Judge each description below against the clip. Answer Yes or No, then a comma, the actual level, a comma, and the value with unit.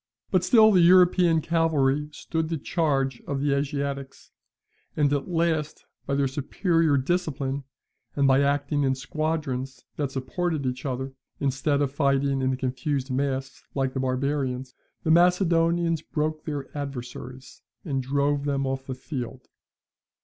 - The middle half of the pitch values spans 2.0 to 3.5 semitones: Yes, average, 3.0 semitones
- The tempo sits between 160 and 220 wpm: No, average, 140 wpm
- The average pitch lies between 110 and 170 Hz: Yes, medium, 140 Hz